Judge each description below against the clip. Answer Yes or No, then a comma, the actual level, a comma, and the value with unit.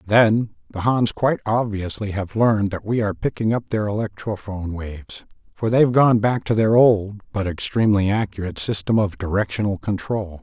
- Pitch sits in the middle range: No, low, 105 Hz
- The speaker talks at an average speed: Yes, average, 165 wpm